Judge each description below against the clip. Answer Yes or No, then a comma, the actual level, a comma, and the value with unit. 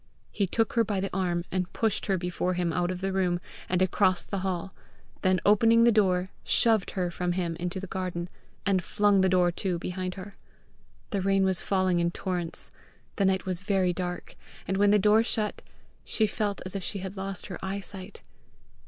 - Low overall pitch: No, high, 190 Hz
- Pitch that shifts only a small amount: Yes, narrow, 1.8 semitones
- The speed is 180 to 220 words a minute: Yes, average, 195 wpm